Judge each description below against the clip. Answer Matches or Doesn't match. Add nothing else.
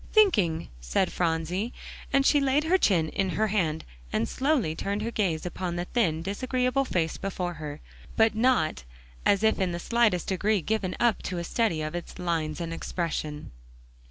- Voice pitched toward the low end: Doesn't match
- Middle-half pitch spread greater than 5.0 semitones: Matches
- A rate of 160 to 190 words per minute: Matches